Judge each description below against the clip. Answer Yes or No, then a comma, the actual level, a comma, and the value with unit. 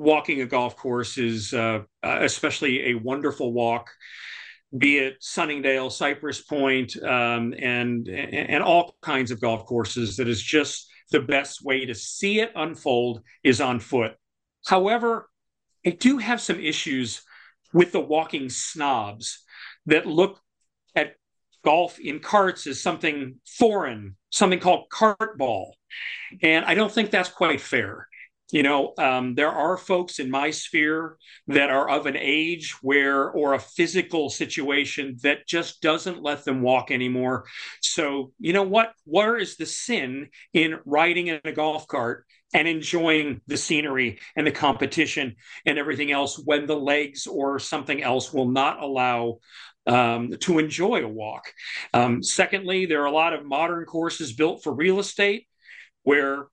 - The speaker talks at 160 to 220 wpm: No, average, 150 wpm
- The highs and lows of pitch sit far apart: No, average, 4.2 semitones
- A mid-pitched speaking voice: Yes, medium, 145 Hz